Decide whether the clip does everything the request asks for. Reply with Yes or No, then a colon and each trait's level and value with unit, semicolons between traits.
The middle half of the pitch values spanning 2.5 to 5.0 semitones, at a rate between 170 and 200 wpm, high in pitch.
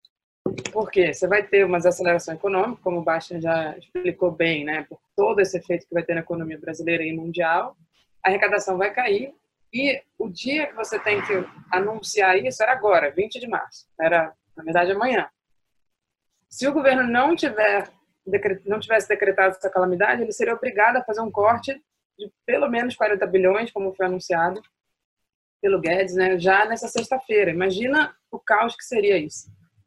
Yes: average, 4.1 semitones; average, 175 wpm; high, 195 Hz